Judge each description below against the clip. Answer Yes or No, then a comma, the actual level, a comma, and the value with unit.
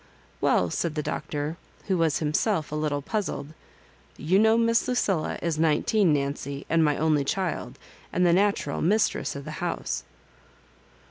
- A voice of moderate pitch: Yes, medium, 160 Hz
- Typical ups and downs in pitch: Yes, average, 4.5 semitones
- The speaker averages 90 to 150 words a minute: No, average, 160 wpm